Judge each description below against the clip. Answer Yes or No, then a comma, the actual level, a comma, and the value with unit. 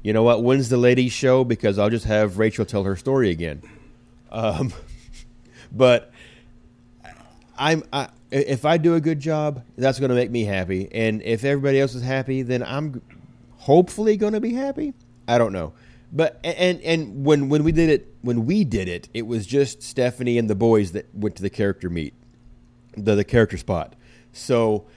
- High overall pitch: No, low, 120 Hz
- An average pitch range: Yes, average, 3.9 semitones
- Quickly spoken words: No, average, 190 wpm